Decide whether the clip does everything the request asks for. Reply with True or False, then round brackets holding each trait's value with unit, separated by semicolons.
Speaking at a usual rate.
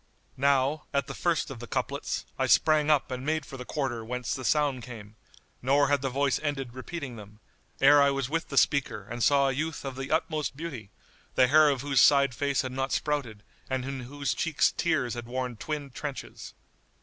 False (210 wpm)